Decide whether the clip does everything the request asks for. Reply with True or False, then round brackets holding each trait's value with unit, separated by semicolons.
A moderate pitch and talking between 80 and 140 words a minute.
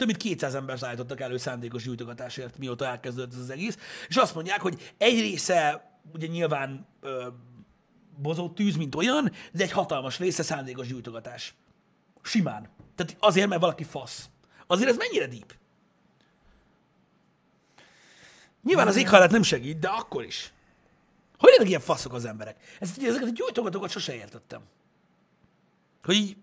False (155 Hz; 150 wpm)